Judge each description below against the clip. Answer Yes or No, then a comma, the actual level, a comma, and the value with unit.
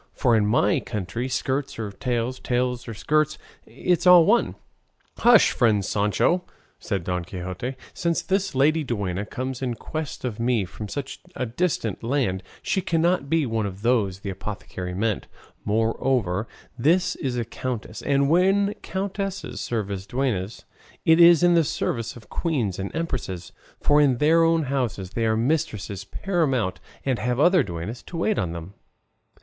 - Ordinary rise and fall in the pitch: No, wide, 7.3 semitones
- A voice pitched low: Yes, low, 125 Hz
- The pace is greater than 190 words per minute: No, average, 160 wpm